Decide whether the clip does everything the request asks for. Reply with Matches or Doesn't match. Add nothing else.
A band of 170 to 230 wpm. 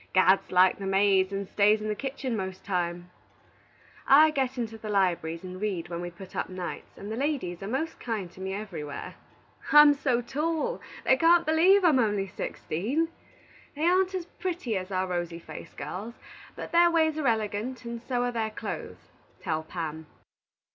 Matches